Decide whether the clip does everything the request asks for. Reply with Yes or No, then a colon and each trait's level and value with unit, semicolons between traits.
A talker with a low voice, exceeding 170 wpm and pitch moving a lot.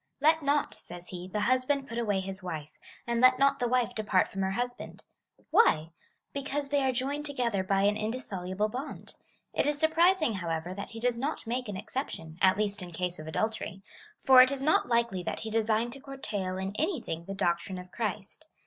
No: high, 220 Hz; fast, 205 wpm; wide, 5.9 semitones